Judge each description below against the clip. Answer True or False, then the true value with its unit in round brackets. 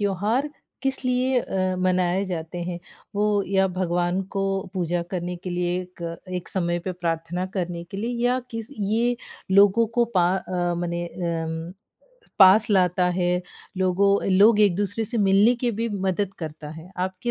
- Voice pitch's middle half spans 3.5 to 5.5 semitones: False (2.7 semitones)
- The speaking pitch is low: False (185 Hz)